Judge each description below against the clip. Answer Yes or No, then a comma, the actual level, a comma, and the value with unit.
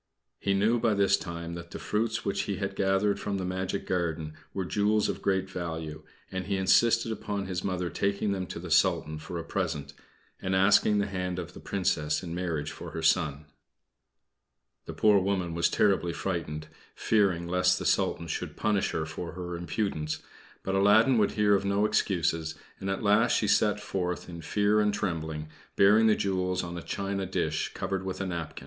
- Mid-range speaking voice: No, very low, 95 Hz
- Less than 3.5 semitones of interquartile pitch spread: Yes, average, 2.9 semitones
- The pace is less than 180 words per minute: No, average, 190 wpm